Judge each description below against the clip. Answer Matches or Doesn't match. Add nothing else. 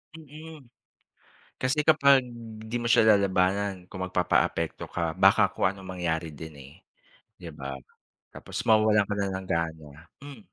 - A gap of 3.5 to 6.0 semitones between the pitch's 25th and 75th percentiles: Matches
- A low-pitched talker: Matches